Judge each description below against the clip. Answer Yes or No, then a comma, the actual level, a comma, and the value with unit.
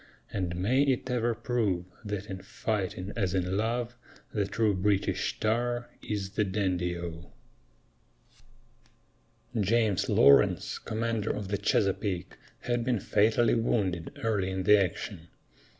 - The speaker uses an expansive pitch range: No, average, 3.5 semitones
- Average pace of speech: No, slow, 125 wpm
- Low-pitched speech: Yes, low, 105 Hz